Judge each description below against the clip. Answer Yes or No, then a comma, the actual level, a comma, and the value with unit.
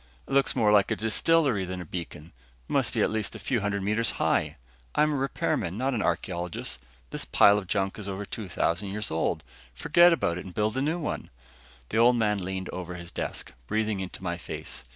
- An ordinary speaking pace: No, fast, 215 wpm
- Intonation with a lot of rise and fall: No, average, 4.0 semitones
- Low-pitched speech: Yes, low, 105 Hz